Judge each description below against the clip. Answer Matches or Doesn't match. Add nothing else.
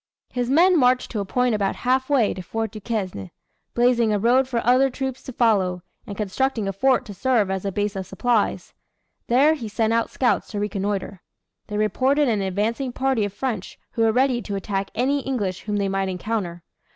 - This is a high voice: Matches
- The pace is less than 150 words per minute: Doesn't match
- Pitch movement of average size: Matches